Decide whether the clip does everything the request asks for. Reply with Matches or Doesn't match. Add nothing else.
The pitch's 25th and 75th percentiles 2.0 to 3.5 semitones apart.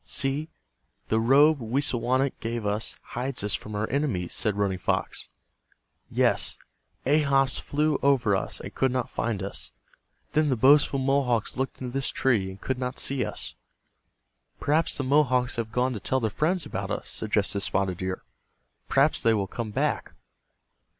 Doesn't match